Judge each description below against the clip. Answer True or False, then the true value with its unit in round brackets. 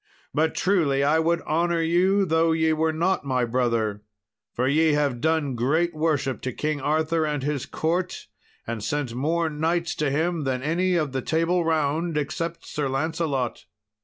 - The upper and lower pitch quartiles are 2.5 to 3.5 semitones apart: True (3.2 semitones)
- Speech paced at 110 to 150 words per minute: False (165 wpm)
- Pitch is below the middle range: False (155 Hz)